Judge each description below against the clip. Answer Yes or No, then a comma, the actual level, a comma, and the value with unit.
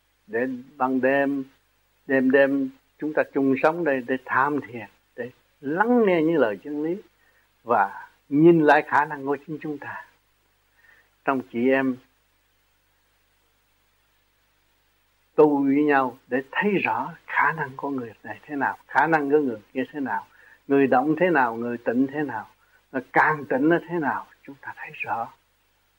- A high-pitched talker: No, low, 135 Hz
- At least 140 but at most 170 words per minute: Yes, slow, 165 wpm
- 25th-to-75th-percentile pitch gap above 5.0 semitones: Yes, wide, 5.6 semitones